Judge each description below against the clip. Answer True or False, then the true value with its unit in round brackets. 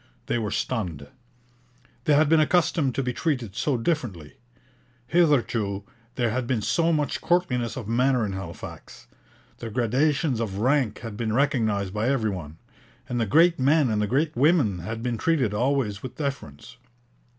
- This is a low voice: True (120 Hz)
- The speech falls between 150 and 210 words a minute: True (160 wpm)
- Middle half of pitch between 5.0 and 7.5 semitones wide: True (5.3 semitones)